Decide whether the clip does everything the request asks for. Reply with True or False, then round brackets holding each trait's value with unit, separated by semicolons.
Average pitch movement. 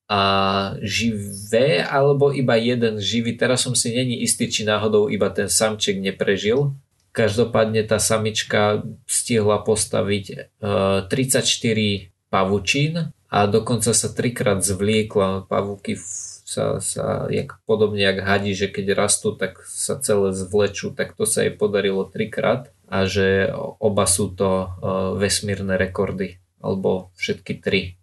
True (3.0 semitones)